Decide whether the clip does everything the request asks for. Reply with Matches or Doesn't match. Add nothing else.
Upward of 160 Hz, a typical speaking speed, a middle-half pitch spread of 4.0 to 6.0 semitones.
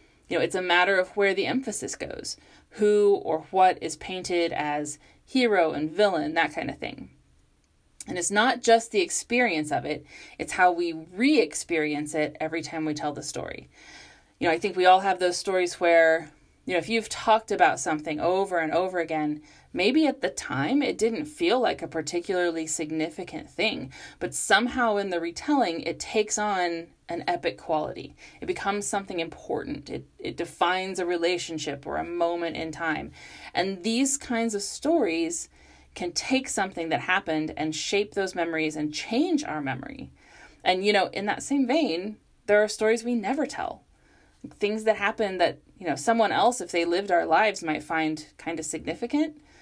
Matches